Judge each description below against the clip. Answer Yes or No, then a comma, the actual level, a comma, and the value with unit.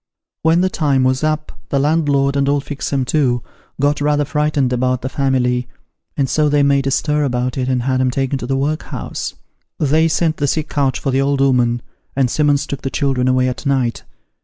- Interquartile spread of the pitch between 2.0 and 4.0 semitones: Yes, narrow, 2.4 semitones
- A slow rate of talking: No, fast, 205 wpm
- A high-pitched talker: No, medium, 140 Hz